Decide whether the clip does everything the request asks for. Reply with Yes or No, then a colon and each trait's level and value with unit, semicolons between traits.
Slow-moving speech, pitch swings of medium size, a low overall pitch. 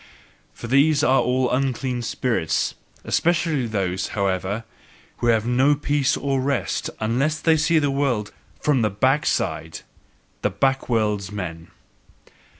Yes: slow, 120 wpm; average, 4.7 semitones; low, 125 Hz